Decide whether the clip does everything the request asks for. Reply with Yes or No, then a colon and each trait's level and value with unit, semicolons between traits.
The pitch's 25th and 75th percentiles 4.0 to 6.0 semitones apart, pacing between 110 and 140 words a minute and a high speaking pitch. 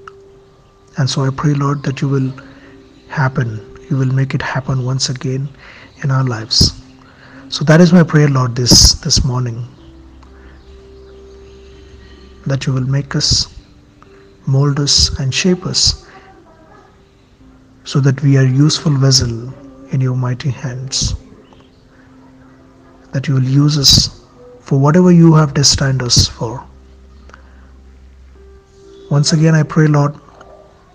No: average, 5.3 semitones; average, 125 wpm; low, 130 Hz